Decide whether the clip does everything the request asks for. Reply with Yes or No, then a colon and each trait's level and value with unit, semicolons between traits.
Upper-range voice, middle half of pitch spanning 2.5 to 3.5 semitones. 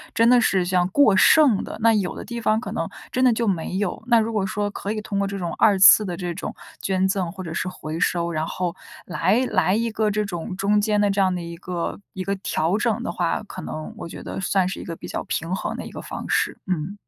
Yes: high, 195 Hz; average, 3.1 semitones